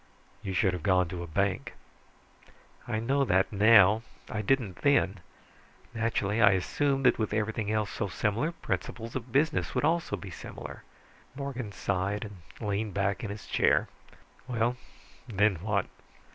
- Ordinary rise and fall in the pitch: Yes, average, 3.1 semitones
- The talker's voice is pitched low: Yes, low, 105 Hz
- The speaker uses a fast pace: No, average, 150 wpm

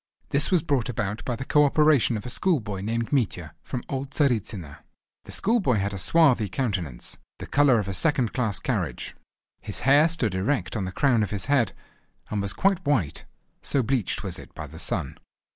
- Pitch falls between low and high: No, low, 125 Hz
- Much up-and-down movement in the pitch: Yes, wide, 6.0 semitones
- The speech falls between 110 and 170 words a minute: No, average, 195 wpm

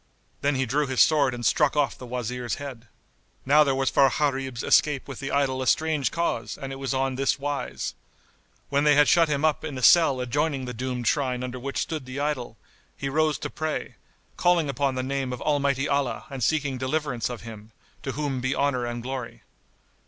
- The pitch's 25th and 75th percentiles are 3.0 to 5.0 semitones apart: No, narrow, 2.4 semitones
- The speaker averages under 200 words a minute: No, fast, 205 wpm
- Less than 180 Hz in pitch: Yes, low, 135 Hz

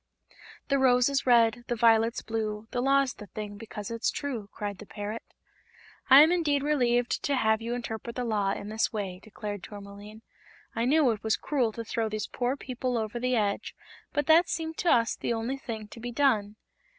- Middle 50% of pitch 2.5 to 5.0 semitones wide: Yes, average, 3.3 semitones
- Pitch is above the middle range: Yes, high, 230 Hz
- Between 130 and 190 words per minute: No, average, 200 wpm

